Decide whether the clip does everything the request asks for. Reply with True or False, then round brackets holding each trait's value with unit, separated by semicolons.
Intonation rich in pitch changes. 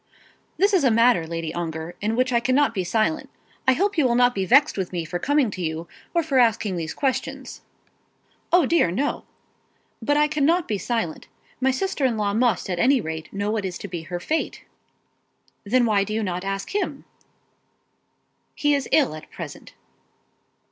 True (7.3 semitones)